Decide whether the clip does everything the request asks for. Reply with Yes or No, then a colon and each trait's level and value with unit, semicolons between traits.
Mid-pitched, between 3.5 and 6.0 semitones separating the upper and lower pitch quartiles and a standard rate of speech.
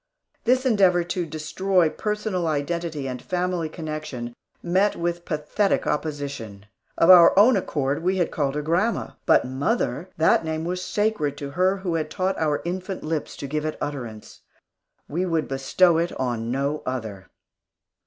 Yes: medium, 160 Hz; average, 4.3 semitones; average, 155 wpm